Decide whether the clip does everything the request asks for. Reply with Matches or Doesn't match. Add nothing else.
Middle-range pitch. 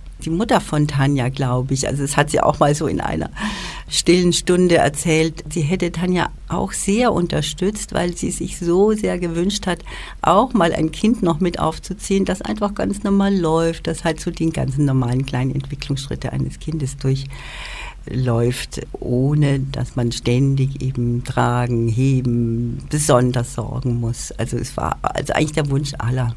Matches